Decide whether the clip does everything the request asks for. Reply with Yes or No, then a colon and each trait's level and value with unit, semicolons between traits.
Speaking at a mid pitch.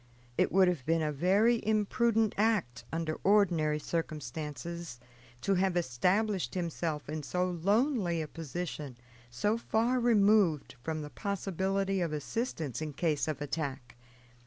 Yes: medium, 170 Hz